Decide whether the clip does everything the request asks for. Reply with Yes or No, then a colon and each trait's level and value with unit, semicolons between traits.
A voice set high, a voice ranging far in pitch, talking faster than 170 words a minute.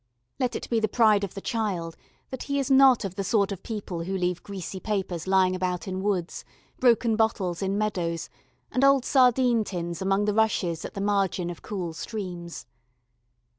No: high, 200 Hz; average, 3.5 semitones; average, 185 wpm